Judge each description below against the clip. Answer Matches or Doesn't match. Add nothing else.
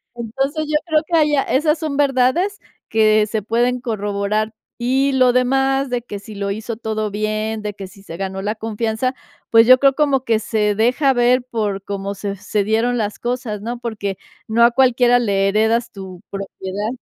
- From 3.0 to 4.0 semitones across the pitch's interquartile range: Matches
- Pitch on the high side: Matches